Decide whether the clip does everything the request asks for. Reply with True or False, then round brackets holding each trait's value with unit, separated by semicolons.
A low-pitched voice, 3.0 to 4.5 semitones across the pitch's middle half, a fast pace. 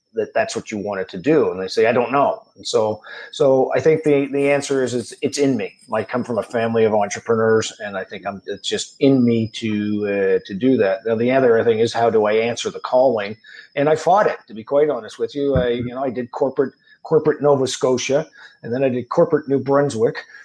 True (130 Hz; 3.8 semitones; 245 wpm)